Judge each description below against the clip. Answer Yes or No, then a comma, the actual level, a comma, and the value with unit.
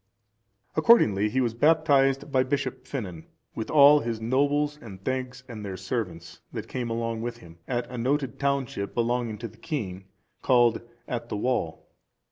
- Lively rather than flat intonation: No, average, 3.7 semitones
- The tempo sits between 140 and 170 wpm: Yes, average, 160 wpm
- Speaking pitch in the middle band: No, low, 120 Hz